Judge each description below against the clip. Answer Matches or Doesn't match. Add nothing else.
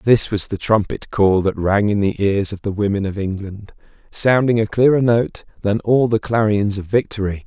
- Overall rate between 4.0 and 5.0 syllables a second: Matches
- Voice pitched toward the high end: Doesn't match